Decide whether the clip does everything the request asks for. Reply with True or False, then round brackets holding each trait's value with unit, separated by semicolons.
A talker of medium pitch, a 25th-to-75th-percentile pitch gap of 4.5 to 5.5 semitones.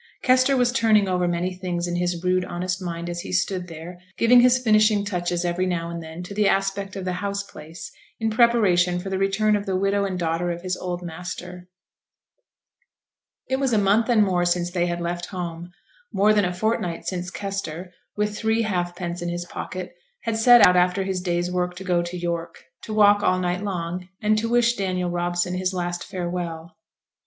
False (180 Hz; 2.6 semitones)